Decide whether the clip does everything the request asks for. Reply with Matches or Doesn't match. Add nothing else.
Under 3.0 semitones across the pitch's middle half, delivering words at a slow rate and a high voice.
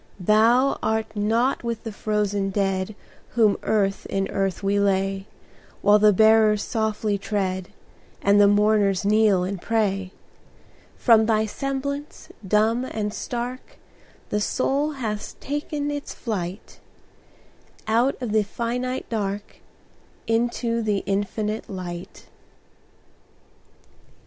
Matches